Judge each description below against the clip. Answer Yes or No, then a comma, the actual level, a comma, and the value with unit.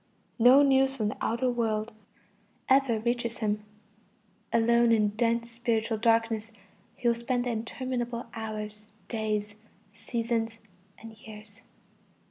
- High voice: Yes, high, 230 Hz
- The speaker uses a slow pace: Yes, slow, 115 wpm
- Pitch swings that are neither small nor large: No, narrow, 1.6 semitones